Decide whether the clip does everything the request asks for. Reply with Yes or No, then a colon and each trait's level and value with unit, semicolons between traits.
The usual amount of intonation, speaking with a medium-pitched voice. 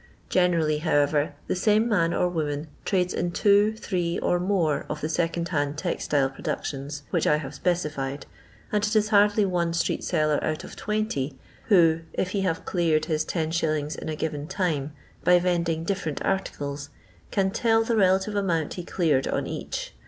Yes: average, 3.9 semitones; medium, 170 Hz